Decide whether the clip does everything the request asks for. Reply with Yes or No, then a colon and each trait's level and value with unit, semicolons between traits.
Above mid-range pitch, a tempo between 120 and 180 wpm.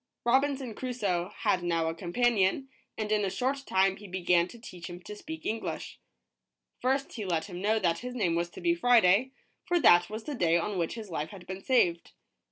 No: high, 205 Hz; fast, 205 wpm